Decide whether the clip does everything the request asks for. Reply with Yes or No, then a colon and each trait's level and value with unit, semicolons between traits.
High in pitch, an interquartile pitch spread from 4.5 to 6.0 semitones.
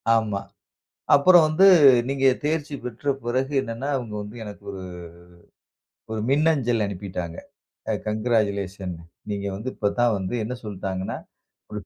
No: low, 110 Hz; average, 5.0 semitones